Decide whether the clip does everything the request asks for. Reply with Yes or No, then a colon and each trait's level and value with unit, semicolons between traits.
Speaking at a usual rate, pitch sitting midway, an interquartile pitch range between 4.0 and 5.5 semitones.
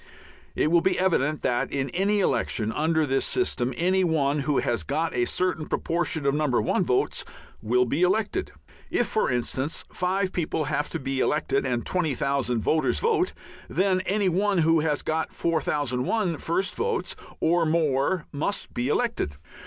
Yes: average, 160 wpm; medium, 160 Hz; average, 5.2 semitones